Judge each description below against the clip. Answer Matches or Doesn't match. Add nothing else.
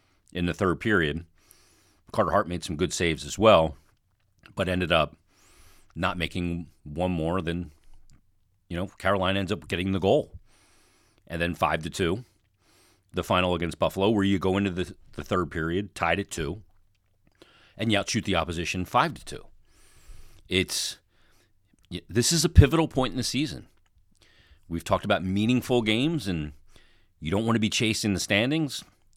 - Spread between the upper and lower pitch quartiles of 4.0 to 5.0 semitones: Doesn't match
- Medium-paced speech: Matches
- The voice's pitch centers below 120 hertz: Matches